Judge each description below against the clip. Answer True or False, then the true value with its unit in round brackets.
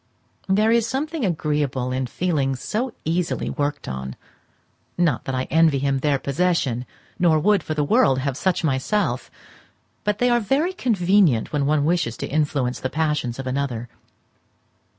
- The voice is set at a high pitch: False (150 Hz)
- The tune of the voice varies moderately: False (6.1 semitones)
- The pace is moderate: True (155 wpm)